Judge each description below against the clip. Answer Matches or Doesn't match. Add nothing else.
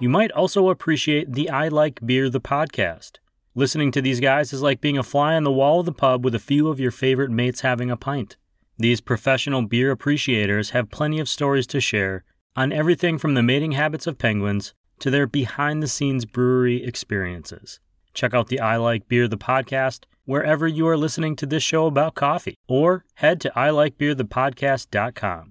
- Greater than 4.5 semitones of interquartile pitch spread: Doesn't match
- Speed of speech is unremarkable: Matches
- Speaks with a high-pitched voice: Doesn't match